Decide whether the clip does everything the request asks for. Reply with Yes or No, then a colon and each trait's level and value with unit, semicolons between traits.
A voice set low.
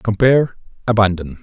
Yes: low, 105 Hz